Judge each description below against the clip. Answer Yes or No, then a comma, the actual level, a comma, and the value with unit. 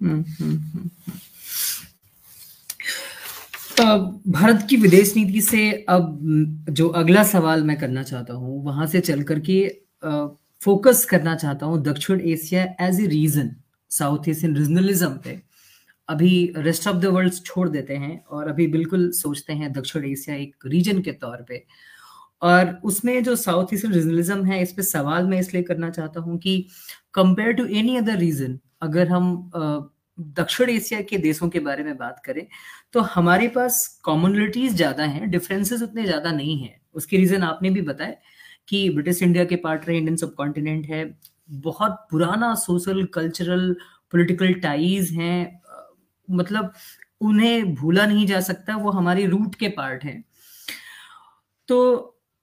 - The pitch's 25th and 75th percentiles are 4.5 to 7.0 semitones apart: No, average, 3.9 semitones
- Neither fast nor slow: Yes, average, 145 wpm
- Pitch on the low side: No, medium, 175 Hz